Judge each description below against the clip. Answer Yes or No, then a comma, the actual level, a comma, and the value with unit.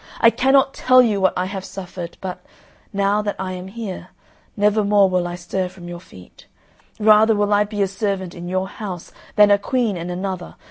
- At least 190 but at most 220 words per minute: Yes, average, 200 wpm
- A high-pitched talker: Yes, high, 195 Hz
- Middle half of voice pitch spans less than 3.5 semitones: Yes, narrow, 2.4 semitones